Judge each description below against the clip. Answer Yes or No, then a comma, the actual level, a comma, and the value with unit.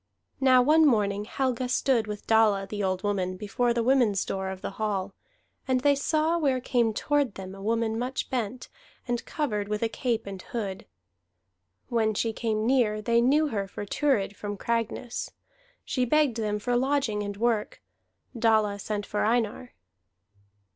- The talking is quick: No, average, 165 wpm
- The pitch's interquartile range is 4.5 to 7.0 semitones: No, average, 3.6 semitones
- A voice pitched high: Yes, high, 225 Hz